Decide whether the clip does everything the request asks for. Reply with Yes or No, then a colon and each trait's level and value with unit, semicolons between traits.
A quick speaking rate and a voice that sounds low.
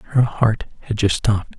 No: average, 190 wpm; low, 110 Hz